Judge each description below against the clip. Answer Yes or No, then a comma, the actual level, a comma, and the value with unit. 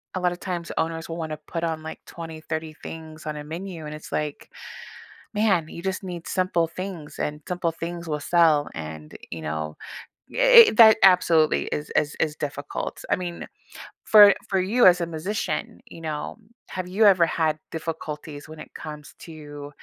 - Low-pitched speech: No, medium, 165 Hz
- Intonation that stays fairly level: No, average, 3.1 semitones